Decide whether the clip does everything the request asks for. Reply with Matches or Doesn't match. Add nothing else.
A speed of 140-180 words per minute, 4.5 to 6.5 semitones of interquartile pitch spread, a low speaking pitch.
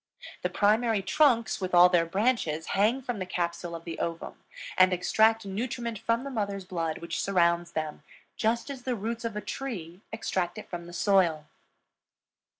Doesn't match